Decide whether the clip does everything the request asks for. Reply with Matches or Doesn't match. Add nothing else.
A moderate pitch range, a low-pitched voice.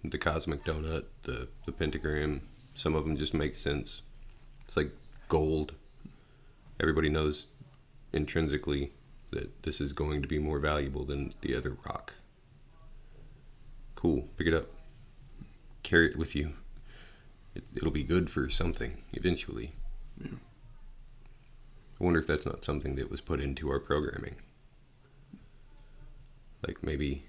Matches